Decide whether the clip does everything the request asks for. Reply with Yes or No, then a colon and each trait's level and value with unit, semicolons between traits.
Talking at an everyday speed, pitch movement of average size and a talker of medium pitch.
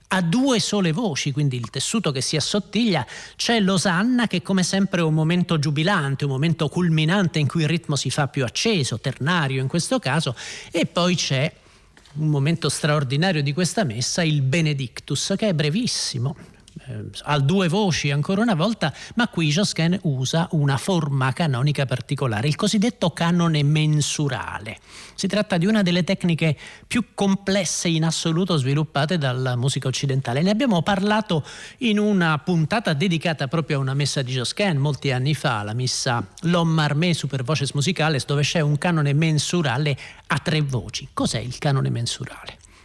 Yes: average, 160 wpm; average, 4.6 semitones; medium, 155 Hz